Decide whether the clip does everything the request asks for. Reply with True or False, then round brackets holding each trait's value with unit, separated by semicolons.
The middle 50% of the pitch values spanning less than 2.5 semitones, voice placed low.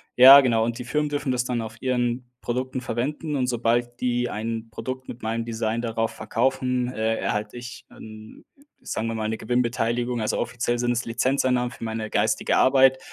True (2.0 semitones; 120 Hz)